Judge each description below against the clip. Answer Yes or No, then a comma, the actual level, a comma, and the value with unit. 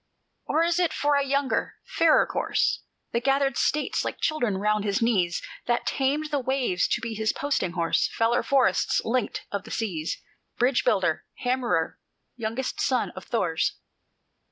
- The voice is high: Yes, high, 240 Hz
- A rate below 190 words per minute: Yes, average, 160 wpm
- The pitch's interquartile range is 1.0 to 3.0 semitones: No, average, 5.0 semitones